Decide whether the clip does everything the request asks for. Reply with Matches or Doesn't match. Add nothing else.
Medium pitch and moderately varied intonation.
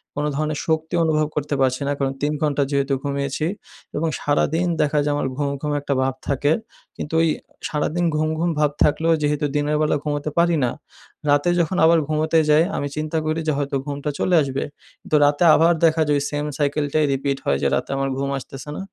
Doesn't match